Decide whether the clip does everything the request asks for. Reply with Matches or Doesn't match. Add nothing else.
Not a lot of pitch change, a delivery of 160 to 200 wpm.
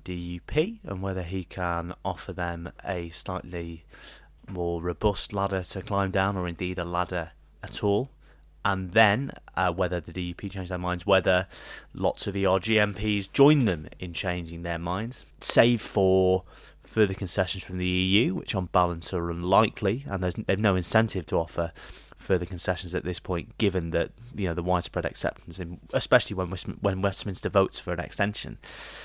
Matches